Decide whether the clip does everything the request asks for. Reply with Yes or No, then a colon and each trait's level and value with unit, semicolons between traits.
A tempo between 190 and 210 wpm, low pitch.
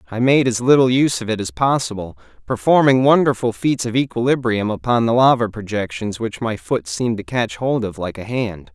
Yes: average, 200 wpm; low, 115 Hz